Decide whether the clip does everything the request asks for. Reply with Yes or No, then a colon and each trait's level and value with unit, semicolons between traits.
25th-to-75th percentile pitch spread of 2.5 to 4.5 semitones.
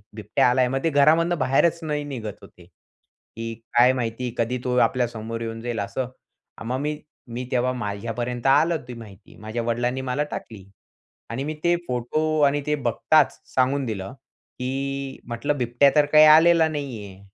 Yes: average, 4.1 semitones